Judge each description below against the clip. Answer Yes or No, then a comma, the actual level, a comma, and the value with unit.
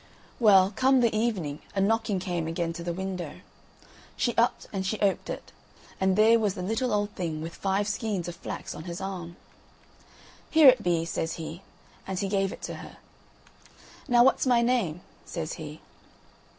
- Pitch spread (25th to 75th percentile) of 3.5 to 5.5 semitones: Yes, average, 4.4 semitones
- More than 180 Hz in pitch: Yes, high, 190 Hz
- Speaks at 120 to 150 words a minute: No, average, 175 wpm